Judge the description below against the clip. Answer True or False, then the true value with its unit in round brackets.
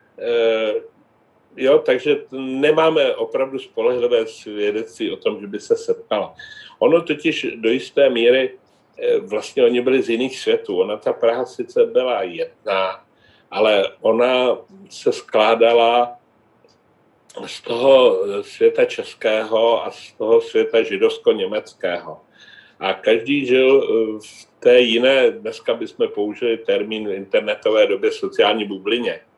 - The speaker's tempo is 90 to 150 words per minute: True (120 wpm)